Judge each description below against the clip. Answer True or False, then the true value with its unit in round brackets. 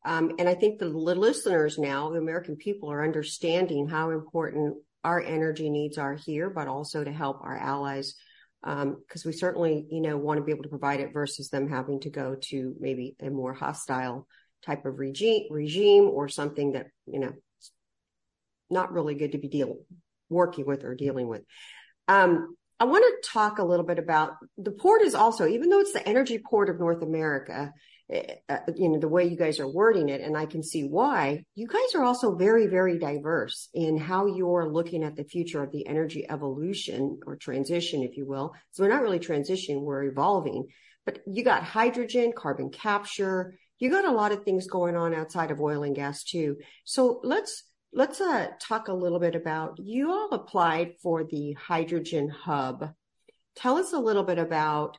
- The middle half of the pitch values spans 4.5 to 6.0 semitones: True (4.8 semitones)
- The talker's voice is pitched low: False (160 Hz)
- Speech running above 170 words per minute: True (195 wpm)